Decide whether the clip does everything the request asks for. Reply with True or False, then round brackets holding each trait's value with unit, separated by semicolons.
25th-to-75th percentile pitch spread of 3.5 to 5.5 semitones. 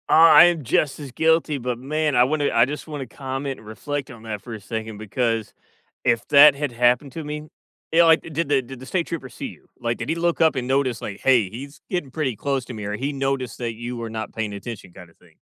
True (4.3 semitones)